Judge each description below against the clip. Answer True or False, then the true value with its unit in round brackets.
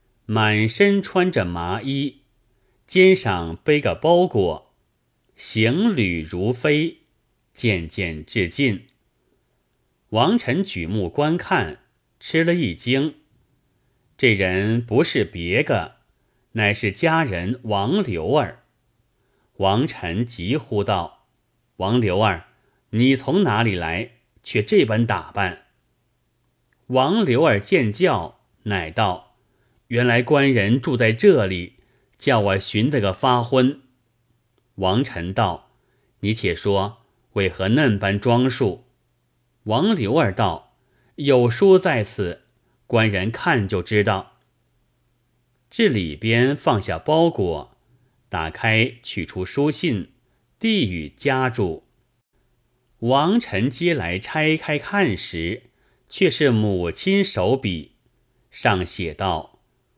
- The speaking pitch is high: False (120 Hz)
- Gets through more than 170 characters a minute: False (145 characters per minute)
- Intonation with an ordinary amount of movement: True (4.9 semitones)